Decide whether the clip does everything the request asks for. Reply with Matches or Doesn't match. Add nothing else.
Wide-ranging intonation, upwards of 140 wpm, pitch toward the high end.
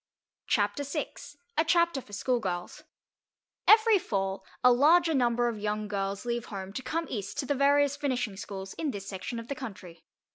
Matches